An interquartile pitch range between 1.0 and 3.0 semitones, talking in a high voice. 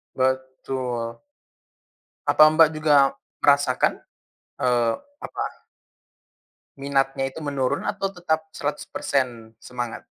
No: average, 2.7 semitones; low, 135 Hz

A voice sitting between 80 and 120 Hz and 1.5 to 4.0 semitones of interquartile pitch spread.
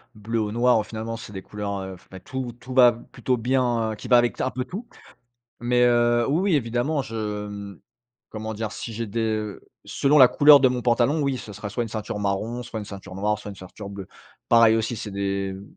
Yes: low, 115 Hz; average, 3.0 semitones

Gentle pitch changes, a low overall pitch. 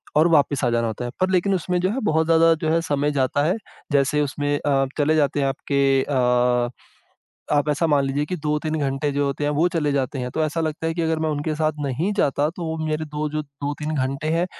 No: narrow, 2.3 semitones; medium, 150 Hz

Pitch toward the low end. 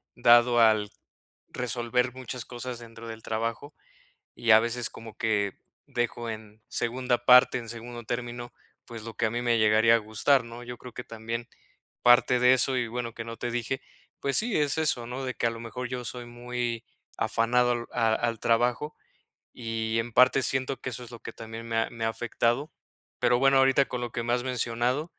Yes: low, 120 Hz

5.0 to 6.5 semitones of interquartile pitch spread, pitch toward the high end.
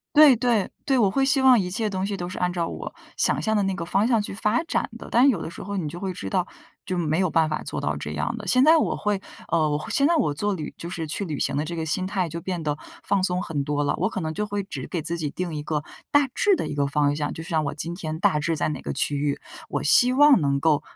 No: average, 5.3 semitones; medium, 180 Hz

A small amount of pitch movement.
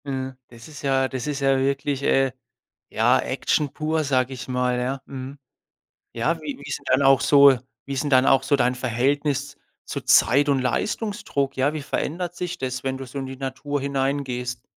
Yes: narrow, 1.6 semitones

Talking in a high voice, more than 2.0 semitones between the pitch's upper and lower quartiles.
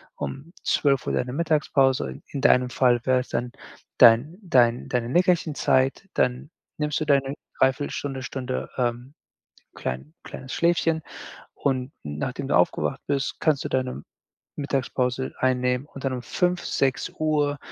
No: low, 135 Hz; average, 2.7 semitones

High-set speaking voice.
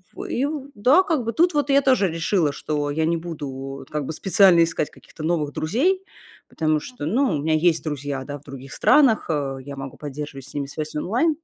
No: medium, 160 Hz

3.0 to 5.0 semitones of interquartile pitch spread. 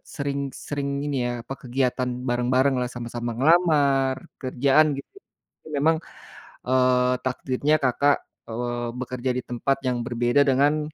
No: narrow, 2.4 semitones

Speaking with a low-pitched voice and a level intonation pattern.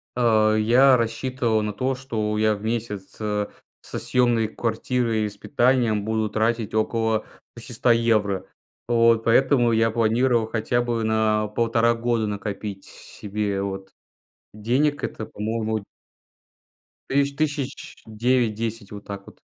Yes: low, 115 Hz; narrow, 2.0 semitones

